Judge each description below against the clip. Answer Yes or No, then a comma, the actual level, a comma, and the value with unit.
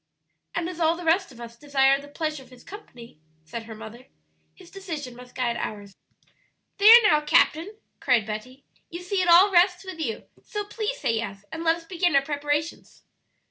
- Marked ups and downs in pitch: Yes, wide, 6.5 semitones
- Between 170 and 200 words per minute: Yes, average, 190 wpm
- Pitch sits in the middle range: No, very high, 300 Hz